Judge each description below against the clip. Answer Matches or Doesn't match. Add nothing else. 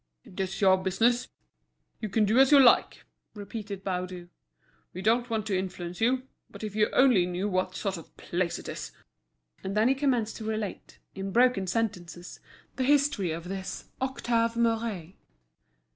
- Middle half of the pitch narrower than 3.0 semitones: Doesn't match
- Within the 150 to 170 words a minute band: Matches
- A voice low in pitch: Doesn't match